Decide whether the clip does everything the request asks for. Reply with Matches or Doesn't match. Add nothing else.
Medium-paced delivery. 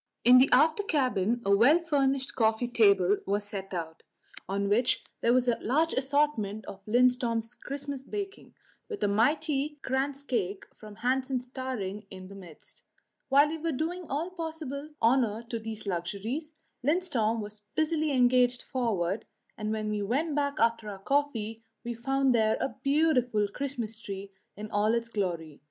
Matches